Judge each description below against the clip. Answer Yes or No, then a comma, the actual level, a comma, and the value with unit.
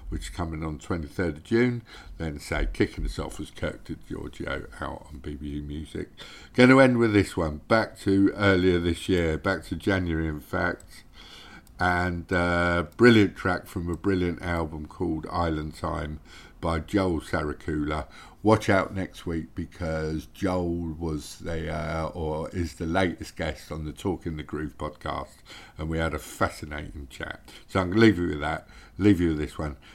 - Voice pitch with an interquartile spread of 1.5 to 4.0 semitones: Yes, average, 3.5 semitones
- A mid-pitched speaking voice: No, very low, 85 Hz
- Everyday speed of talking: Yes, average, 180 wpm